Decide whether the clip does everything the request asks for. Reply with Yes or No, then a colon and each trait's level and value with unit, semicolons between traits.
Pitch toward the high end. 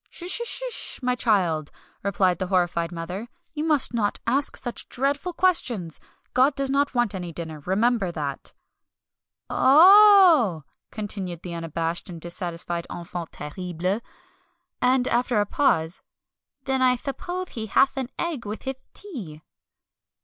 Yes: high, 215 Hz